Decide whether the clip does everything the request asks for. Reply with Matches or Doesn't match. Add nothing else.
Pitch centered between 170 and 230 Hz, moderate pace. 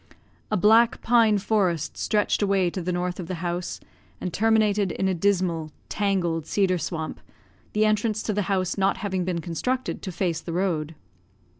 Matches